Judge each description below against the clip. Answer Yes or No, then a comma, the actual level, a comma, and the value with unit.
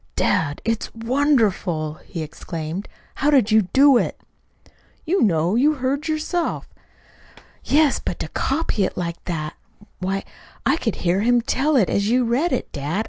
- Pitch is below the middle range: No, high, 225 Hz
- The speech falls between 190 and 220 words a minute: No, average, 155 wpm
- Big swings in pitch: Yes, wide, 8.0 semitones